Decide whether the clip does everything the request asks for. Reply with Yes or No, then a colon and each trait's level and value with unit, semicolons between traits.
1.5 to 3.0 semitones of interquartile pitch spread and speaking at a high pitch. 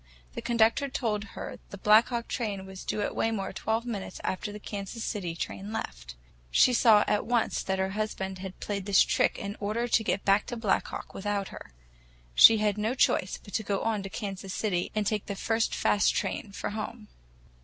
Yes: narrow, 2.4 semitones; high, 210 Hz